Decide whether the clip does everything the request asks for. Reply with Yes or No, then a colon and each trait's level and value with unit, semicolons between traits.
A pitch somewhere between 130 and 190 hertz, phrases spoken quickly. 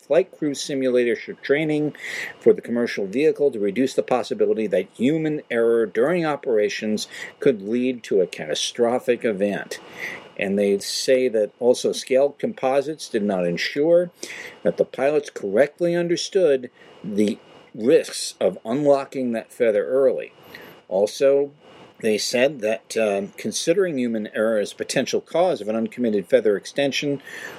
No: medium, 140 Hz; slow, 135 wpm